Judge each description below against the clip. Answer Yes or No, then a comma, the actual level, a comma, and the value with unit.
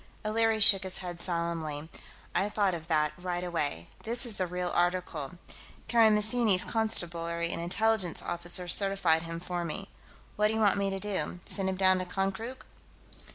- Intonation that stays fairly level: No, average, 3.6 semitones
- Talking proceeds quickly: No, average, 165 wpm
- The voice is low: No, medium, 185 Hz